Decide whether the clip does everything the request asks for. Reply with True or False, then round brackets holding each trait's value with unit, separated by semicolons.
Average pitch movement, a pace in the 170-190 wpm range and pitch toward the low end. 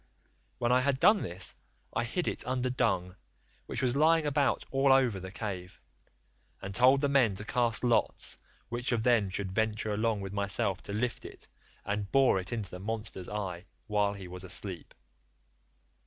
True (4.7 semitones; 175 wpm; 110 Hz)